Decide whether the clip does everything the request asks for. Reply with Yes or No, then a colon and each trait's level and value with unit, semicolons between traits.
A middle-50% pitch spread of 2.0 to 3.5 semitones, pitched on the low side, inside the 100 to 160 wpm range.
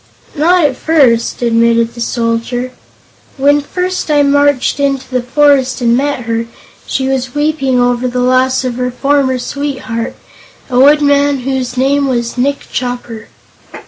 No: average, 2.7 semitones; very high, 260 Hz; average, 145 wpm